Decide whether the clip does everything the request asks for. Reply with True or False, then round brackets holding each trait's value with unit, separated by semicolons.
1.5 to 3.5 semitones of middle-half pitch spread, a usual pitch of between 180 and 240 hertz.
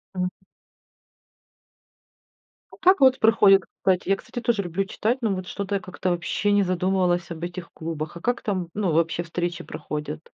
True (2.9 semitones; 185 Hz)